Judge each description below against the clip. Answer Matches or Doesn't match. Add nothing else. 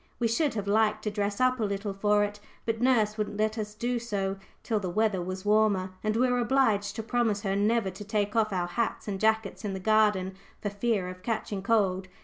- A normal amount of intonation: Doesn't match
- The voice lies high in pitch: Matches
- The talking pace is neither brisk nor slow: Doesn't match